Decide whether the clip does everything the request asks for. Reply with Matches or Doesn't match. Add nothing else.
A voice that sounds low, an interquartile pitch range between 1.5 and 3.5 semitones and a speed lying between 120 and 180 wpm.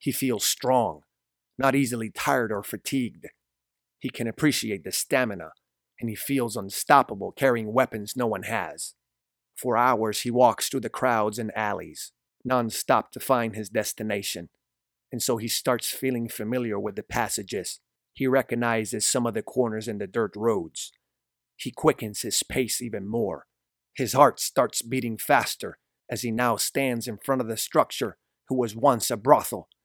Matches